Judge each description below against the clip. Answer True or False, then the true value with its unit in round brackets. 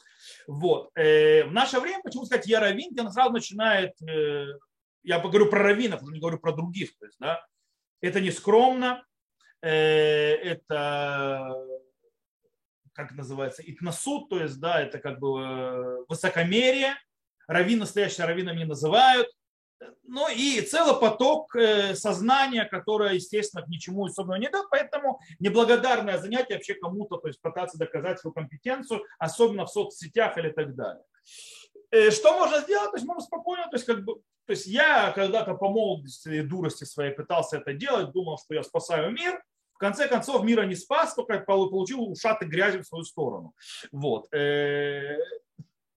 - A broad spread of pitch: True (7.8 semitones)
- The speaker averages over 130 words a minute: True (150 wpm)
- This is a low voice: False (200 Hz)